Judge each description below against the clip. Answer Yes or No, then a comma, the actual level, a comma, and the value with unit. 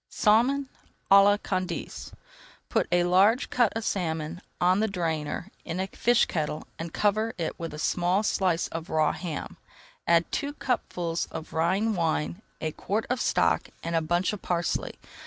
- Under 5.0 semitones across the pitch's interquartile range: Yes, average, 4.2 semitones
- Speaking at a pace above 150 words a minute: Yes, average, 165 wpm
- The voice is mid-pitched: Yes, medium, 180 Hz